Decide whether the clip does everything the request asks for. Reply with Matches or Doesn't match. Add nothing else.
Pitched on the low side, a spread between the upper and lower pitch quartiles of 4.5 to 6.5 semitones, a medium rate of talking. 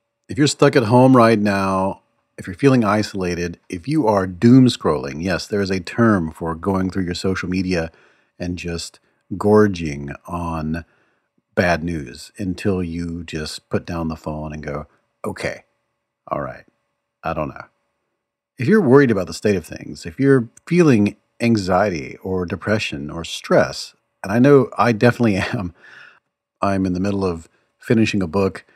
Matches